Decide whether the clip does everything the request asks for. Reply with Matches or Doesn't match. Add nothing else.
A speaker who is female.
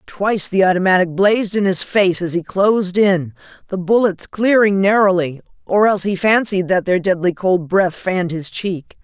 Matches